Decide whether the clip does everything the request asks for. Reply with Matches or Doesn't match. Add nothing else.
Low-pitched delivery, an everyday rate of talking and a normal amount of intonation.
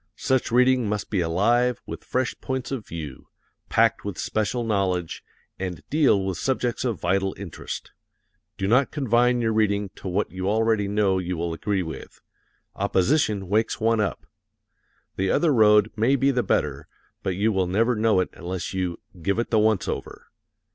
Matches